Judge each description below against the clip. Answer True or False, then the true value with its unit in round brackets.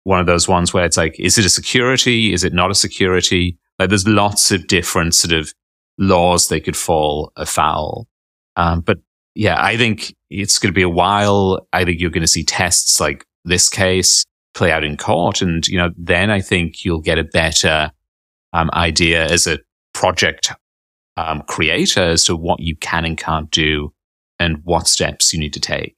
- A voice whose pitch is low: True (85 Hz)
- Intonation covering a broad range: False (2.8 semitones)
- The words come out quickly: False (195 wpm)